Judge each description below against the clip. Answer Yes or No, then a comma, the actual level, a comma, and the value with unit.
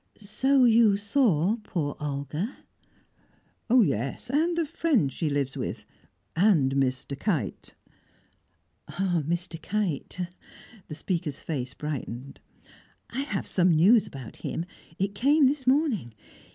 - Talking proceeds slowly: Yes, slow, 110 wpm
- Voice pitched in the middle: Yes, medium, 180 Hz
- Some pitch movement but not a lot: No, wide, 8.8 semitones